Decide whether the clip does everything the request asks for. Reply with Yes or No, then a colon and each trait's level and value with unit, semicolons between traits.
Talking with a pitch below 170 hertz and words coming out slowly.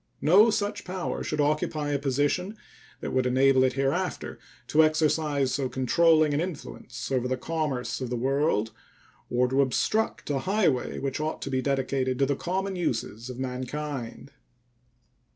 No: medium, 140 Hz; average, 155 wpm